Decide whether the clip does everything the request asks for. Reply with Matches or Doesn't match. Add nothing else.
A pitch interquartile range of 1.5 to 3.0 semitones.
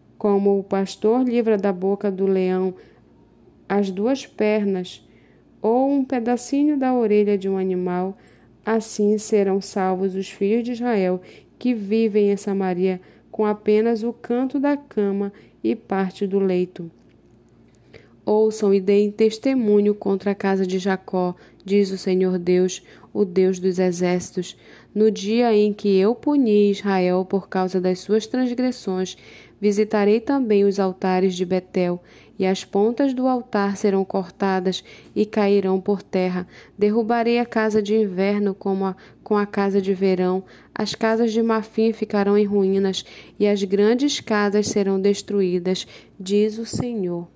Matches